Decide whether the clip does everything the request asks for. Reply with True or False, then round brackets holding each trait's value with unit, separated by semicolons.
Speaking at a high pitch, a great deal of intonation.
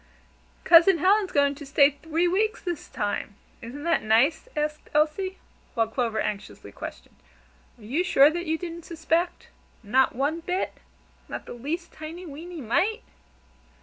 False (315 Hz; 4.3 semitones)